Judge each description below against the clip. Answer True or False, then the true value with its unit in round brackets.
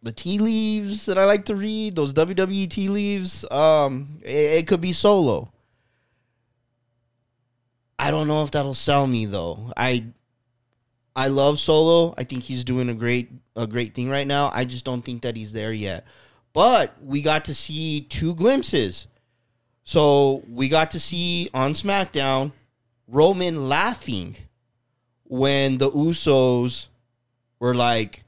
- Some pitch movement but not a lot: True (4.7 semitones)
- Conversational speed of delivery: True (150 wpm)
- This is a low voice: True (130 Hz)